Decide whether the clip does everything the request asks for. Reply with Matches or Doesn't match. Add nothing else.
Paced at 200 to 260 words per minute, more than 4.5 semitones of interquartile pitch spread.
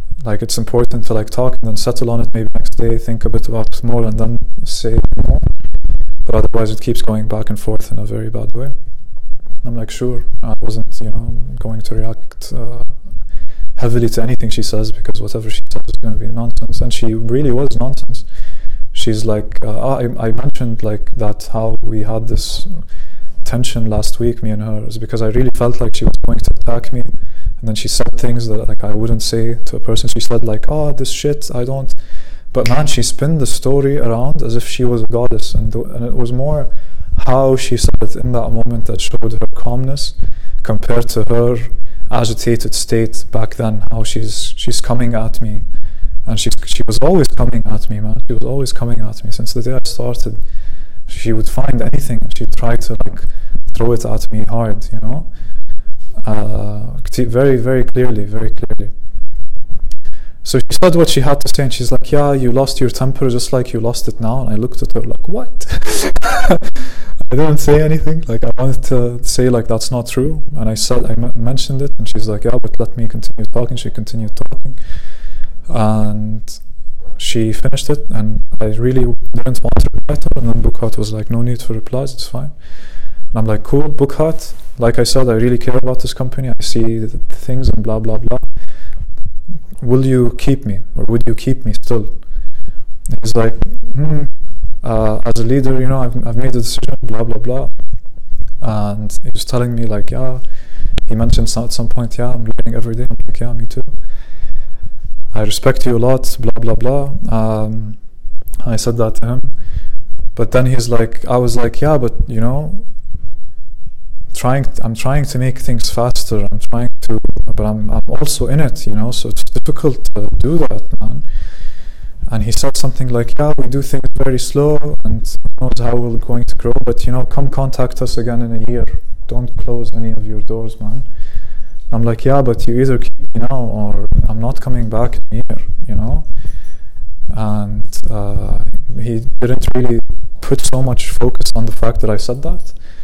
Doesn't match